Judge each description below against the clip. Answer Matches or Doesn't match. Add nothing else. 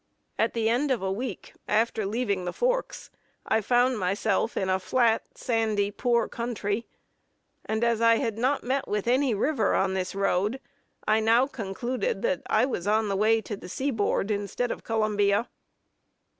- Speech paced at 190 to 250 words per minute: Doesn't match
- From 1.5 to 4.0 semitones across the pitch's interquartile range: Matches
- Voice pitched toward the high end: Matches